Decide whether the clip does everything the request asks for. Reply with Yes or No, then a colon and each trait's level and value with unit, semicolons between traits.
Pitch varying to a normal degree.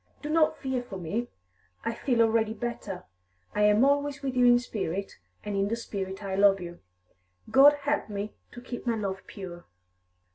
Yes: average, 4.0 semitones